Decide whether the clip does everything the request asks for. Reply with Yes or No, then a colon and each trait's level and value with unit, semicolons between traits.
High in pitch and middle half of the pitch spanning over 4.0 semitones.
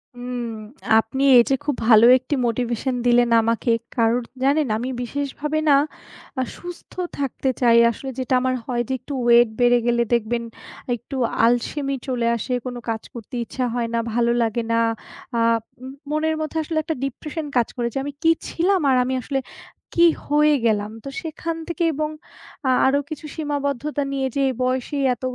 No: very high, 255 Hz; average, 3.5 semitones